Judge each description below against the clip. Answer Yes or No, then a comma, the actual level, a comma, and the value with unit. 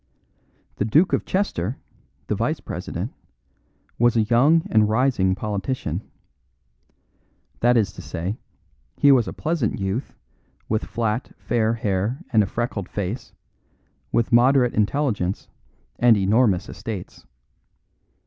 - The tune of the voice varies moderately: Yes, average, 3.7 semitones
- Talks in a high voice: No, low, 115 Hz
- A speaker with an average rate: No, slow, 120 wpm